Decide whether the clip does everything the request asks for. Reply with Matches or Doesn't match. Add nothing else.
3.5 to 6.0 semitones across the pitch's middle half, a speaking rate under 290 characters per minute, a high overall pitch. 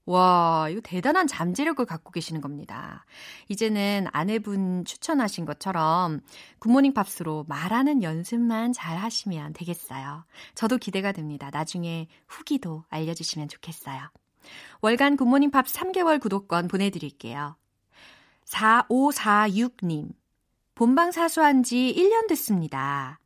Doesn't match